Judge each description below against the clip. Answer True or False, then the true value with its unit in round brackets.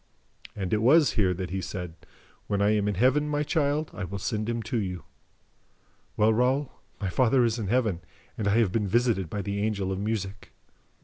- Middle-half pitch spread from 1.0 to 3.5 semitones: False (4.0 semitones)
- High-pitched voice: False (105 Hz)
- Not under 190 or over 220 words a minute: True (200 wpm)